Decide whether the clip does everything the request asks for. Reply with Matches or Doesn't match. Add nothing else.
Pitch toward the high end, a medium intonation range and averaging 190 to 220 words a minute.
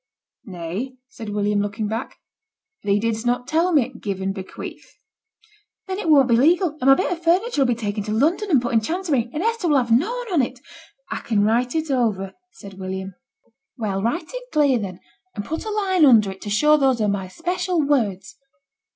Doesn't match